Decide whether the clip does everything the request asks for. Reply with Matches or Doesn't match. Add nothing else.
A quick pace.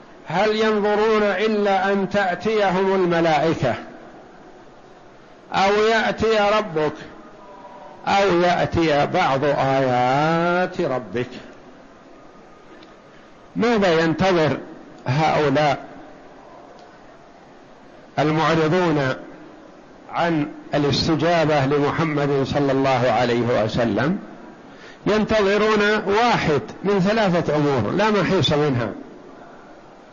Doesn't match